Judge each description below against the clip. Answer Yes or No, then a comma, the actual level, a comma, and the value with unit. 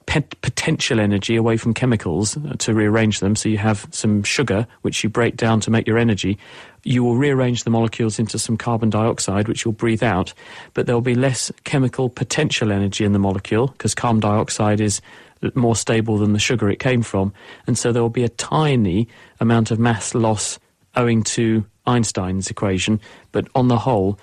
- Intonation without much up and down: Yes, narrow, 2.3 semitones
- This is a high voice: No, low, 115 Hz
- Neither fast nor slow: Yes, average, 185 wpm